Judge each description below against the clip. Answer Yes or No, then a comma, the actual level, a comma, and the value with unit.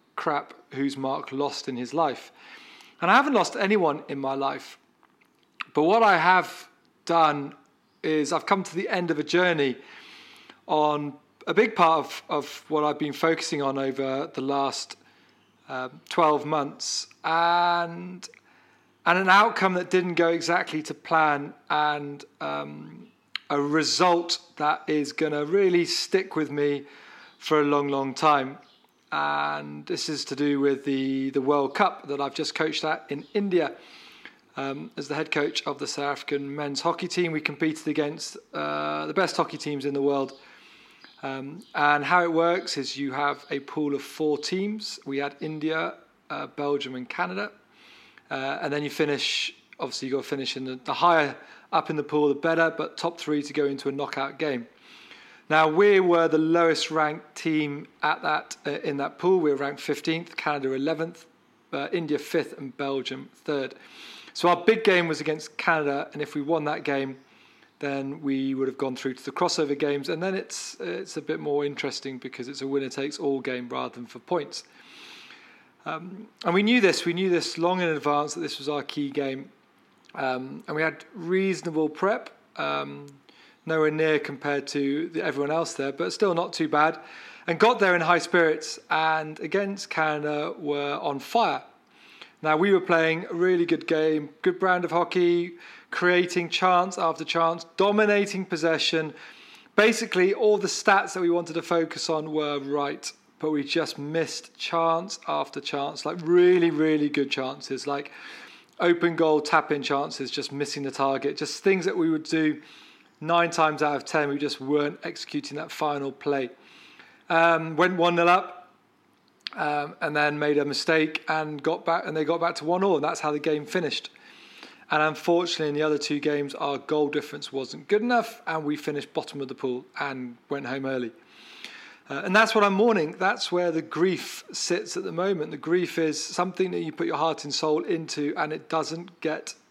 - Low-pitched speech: No, medium, 155 Hz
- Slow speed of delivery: No, average, 185 wpm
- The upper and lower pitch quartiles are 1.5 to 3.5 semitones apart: Yes, average, 3.1 semitones